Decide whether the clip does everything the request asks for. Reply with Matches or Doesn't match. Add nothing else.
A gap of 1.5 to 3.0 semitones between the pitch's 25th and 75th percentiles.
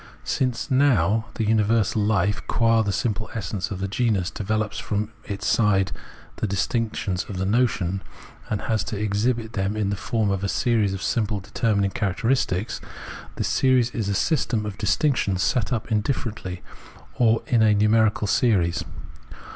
Matches